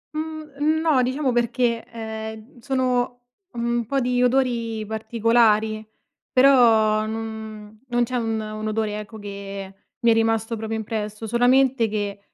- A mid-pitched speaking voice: No, high, 225 Hz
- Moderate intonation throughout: No, narrow, 2.3 semitones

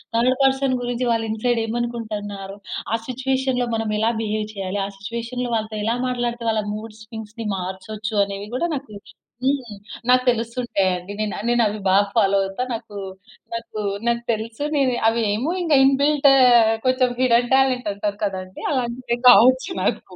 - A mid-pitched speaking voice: No, high, 230 Hz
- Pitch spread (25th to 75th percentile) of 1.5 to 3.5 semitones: Yes, average, 3.0 semitones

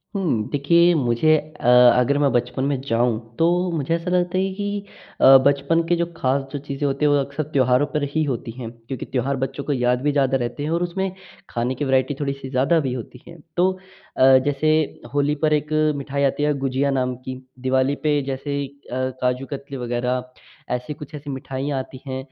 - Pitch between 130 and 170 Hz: Yes, medium, 140 Hz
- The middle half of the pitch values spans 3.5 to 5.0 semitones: No, narrow, 2.5 semitones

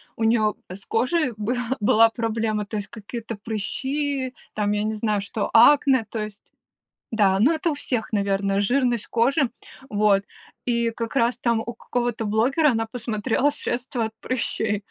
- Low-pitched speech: No, high, 225 Hz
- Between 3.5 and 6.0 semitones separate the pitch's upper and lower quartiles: No, average, 2.9 semitones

